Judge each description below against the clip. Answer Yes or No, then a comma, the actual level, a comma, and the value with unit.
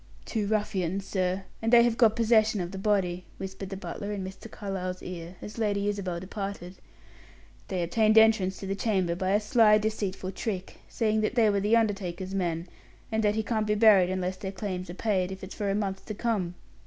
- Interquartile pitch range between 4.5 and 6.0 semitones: No, narrow, 2.5 semitones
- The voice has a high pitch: Yes, high, 200 Hz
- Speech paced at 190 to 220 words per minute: Yes, fast, 205 wpm